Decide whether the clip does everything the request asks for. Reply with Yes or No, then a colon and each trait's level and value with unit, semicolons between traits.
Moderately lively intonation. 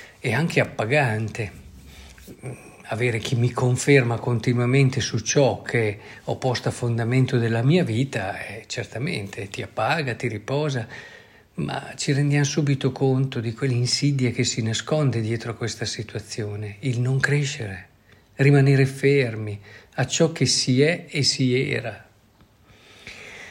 Yes: average, 3.7 semitones